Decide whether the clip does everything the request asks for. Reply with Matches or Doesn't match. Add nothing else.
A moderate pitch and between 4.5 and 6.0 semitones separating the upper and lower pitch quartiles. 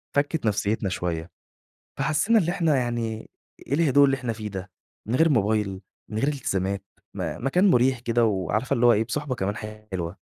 Doesn't match